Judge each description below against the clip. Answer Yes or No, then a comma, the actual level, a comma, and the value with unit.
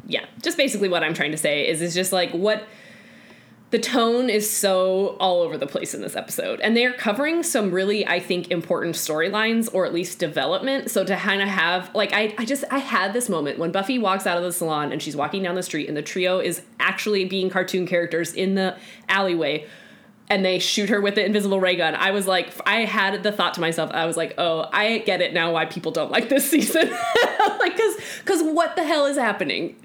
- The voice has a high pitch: Yes, high, 195 Hz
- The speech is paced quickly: Yes, fast, 230 wpm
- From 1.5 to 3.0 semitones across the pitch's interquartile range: No, average, 4.6 semitones